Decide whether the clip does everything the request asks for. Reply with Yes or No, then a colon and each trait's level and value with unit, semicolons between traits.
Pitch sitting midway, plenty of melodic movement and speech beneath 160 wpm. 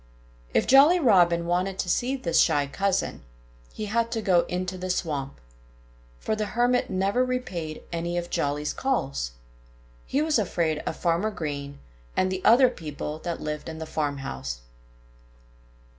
Yes: medium, 180 Hz; wide, 5.9 semitones; average, 150 wpm